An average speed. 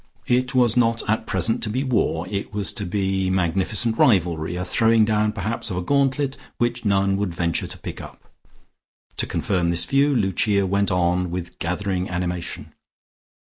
Yes: average, 170 wpm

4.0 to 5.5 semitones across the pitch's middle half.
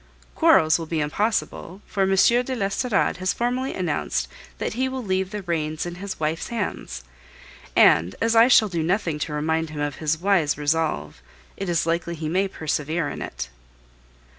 Yes: average, 4.5 semitones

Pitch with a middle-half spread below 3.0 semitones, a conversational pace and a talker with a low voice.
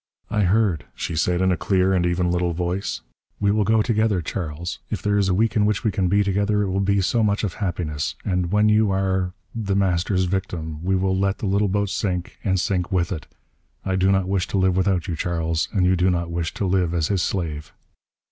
No: narrow, 2.4 semitones; fast, 235 wpm; very low, 95 Hz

